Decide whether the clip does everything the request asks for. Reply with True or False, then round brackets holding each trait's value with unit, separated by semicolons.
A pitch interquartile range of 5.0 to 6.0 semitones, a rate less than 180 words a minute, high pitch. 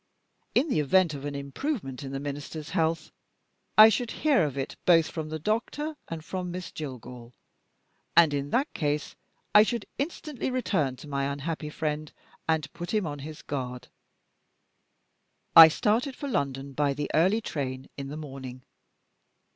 False (5.3 semitones; 160 wpm; 155 Hz)